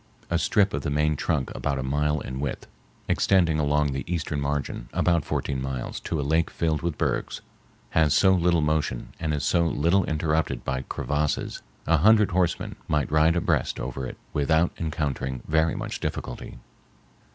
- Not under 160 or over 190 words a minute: Yes, average, 170 wpm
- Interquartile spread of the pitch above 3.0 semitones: No, average, 2.7 semitones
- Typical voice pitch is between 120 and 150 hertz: No, very low, 75 Hz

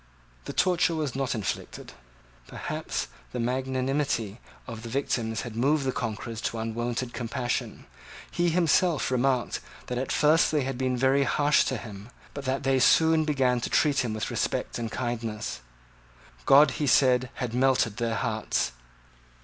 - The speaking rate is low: No, average, 155 wpm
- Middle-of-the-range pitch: No, low, 130 Hz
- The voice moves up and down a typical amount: Yes, average, 3.0 semitones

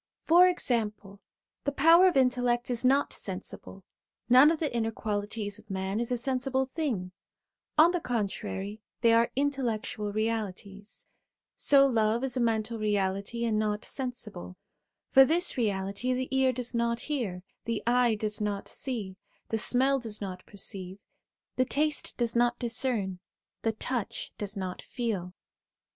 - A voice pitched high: Yes, high, 230 Hz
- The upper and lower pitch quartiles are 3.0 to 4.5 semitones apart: Yes, average, 3.8 semitones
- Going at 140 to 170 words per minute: Yes, average, 150 wpm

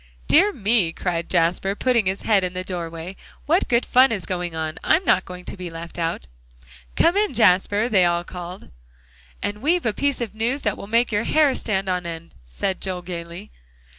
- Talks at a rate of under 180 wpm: No, average, 195 wpm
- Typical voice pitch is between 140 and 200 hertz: Yes, high, 190 Hz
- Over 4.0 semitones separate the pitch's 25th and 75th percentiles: Yes, average, 5.0 semitones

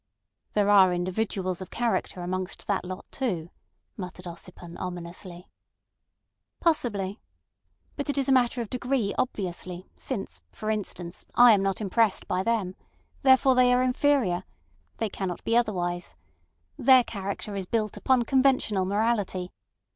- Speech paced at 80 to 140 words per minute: Yes, slow, 135 wpm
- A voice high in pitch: Yes, high, 200 Hz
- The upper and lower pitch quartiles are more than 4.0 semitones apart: Yes, average, 4.8 semitones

